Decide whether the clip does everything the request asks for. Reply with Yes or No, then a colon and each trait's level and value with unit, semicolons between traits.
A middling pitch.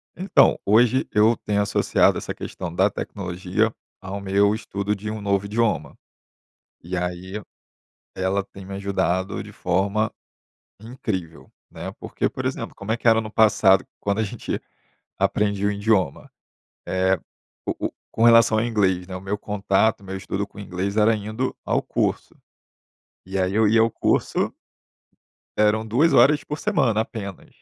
No: low, 100 Hz